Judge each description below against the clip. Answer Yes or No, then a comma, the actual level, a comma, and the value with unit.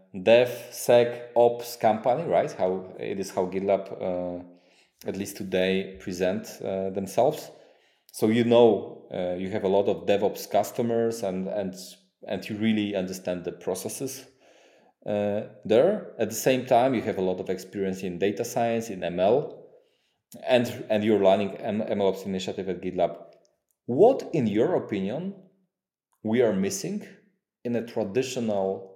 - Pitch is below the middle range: Yes, low, 110 Hz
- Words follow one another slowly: No, average, 145 wpm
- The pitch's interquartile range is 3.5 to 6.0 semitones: Yes, average, 4.3 semitones